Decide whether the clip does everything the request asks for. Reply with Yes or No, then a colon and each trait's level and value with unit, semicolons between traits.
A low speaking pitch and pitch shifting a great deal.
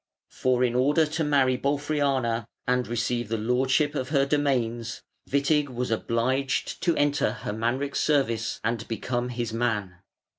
No: low, 125 Hz; average, 3.3 semitones